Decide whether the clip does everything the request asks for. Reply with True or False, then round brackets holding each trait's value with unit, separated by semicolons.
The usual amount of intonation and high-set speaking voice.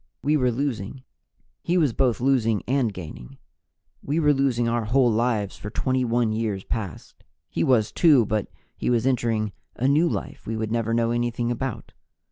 False (3.3 semitones; 120 Hz)